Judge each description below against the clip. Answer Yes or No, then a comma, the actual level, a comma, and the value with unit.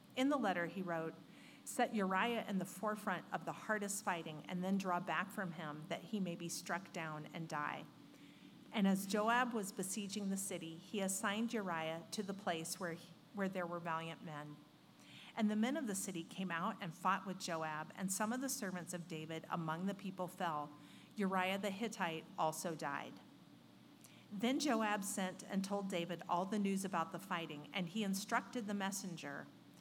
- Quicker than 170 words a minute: Yes, average, 185 wpm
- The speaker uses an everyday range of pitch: Yes, average, 3.6 semitones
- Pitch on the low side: No, medium, 185 Hz